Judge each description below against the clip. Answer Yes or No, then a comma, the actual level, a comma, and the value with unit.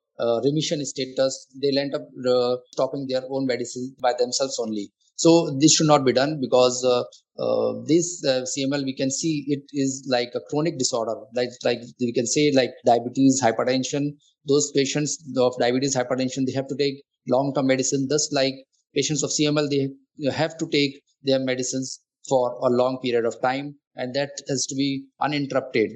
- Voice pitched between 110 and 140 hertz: Yes, low, 135 Hz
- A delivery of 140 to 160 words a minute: No, average, 180 wpm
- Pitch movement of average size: No, narrow, 2.0 semitones